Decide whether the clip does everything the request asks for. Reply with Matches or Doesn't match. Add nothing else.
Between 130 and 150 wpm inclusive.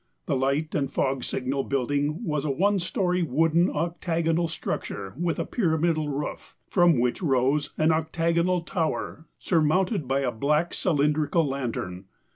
Matches